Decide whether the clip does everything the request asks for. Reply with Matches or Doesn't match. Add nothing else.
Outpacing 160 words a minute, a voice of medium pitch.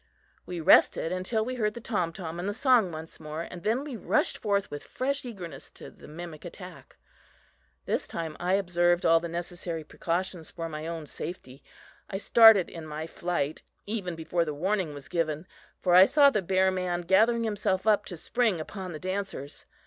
Matches